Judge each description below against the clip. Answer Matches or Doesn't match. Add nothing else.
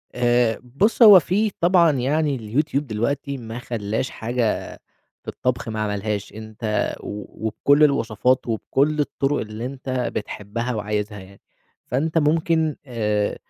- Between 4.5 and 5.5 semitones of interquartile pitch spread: Matches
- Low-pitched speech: Matches